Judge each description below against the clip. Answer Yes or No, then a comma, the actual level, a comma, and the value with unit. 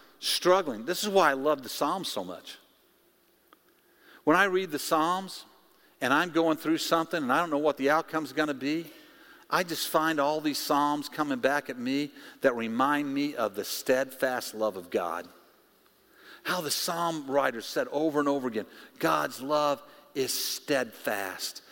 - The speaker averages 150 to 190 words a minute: Yes, average, 175 wpm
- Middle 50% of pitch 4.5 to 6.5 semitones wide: No, narrow, 2.6 semitones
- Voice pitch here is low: No, medium, 150 Hz